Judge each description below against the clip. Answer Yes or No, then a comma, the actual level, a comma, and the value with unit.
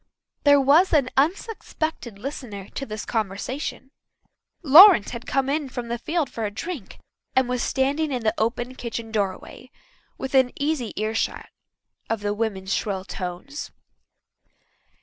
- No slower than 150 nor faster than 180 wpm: No, slow, 135 wpm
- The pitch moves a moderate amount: Yes, average, 4.7 semitones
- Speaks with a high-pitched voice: Yes, very high, 250 Hz